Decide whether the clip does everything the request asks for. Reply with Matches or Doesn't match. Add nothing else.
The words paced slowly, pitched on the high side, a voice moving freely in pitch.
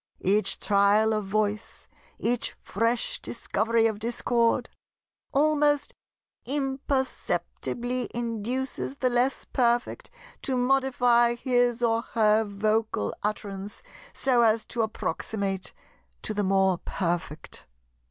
Doesn't match